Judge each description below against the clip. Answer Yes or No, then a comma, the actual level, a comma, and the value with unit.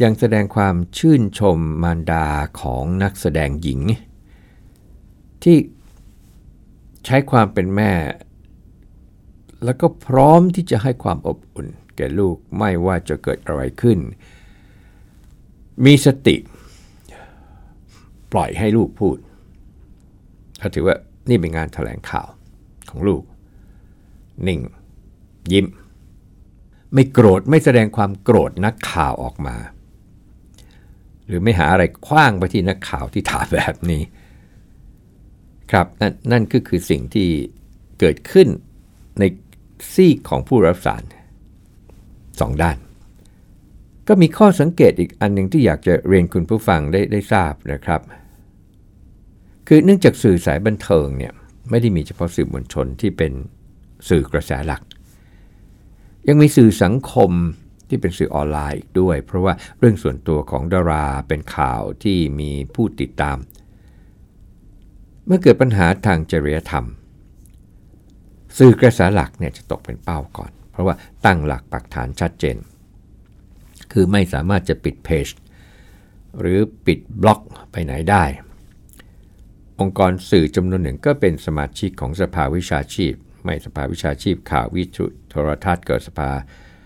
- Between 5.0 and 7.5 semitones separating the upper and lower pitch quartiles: No, average, 4.2 semitones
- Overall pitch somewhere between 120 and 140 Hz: No, very low, 95 Hz